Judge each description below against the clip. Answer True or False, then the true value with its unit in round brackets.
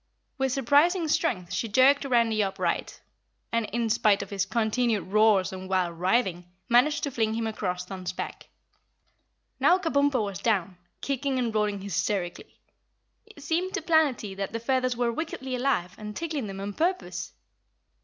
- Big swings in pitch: True (5.7 semitones)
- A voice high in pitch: True (230 Hz)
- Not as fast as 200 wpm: True (155 wpm)